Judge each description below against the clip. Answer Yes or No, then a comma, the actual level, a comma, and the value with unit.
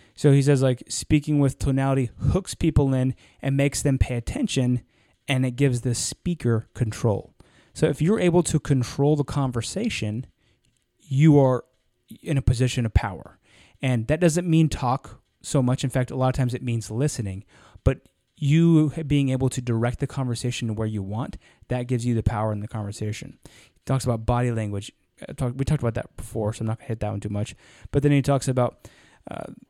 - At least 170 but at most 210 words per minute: Yes, average, 200 wpm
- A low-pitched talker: Yes, low, 125 Hz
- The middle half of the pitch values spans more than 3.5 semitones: Yes, average, 3.9 semitones